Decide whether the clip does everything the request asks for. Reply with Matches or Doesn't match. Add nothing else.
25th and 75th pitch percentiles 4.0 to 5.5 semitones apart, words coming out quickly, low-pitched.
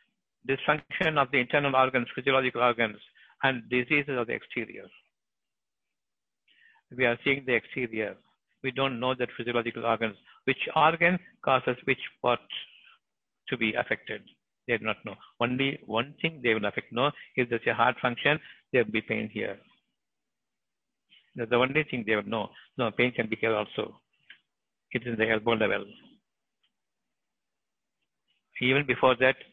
Doesn't match